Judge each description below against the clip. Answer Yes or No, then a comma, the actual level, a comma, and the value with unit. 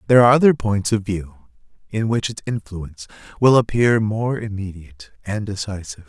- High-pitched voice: No, low, 105 Hz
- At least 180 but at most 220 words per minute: No, average, 160 wpm